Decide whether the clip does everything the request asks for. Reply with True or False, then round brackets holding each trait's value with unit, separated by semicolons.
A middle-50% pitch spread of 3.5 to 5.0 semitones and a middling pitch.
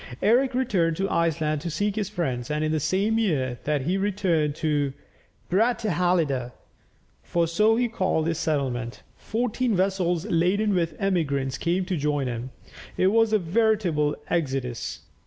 False (5.4 semitones; 170 Hz)